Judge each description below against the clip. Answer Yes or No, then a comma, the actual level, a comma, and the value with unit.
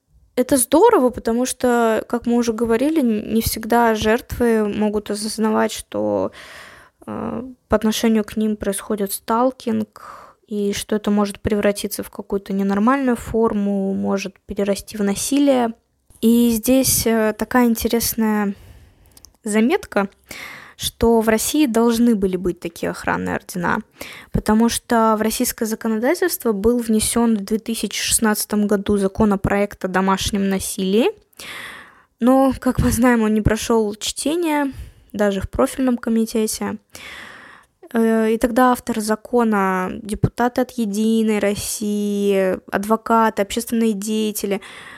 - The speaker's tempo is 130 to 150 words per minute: No, average, 115 wpm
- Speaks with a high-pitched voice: Yes, high, 220 Hz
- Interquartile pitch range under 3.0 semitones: Yes, narrow, 2.4 semitones